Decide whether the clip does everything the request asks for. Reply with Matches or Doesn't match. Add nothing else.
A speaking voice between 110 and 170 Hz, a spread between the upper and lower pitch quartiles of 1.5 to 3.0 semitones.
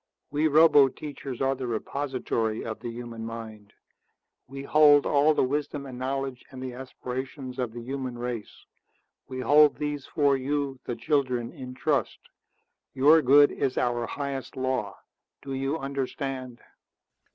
Matches